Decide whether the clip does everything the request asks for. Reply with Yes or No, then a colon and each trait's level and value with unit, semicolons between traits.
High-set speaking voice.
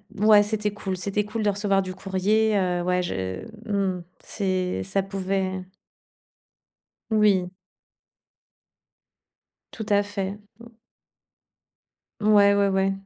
Yes: high, 195 Hz